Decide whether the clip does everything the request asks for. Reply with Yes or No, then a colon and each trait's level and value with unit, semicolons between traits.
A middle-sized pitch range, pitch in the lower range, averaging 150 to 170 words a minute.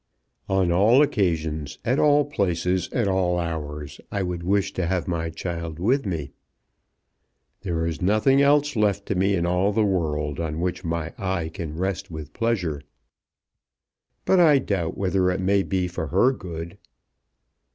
Yes: average, 3.5 semitones; very low, 90 Hz; average, 160 wpm